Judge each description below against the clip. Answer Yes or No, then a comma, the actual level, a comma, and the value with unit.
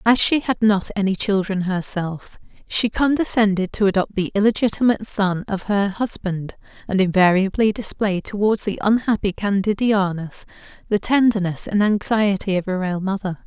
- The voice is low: No, high, 200 Hz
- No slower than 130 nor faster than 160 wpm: Yes, average, 145 wpm